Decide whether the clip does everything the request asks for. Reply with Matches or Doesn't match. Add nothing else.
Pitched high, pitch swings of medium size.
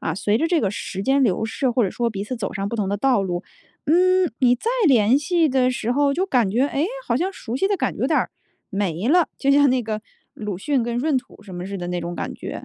Doesn't match